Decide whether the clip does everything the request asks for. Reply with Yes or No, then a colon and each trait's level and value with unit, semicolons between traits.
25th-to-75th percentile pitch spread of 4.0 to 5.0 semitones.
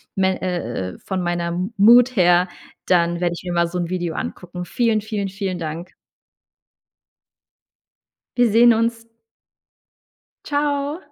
Yes: average, 4.7 semitones